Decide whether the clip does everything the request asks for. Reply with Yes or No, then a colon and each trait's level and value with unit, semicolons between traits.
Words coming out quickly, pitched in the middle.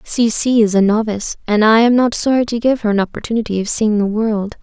No: fast, 245 wpm; high, 220 Hz